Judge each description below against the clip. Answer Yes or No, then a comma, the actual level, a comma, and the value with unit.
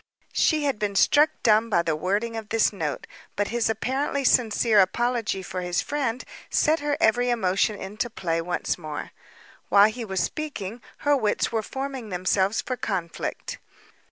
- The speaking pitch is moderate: No, high, 220 Hz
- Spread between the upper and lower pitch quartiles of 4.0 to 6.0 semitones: Yes, average, 4.7 semitones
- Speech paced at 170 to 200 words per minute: No, average, 160 wpm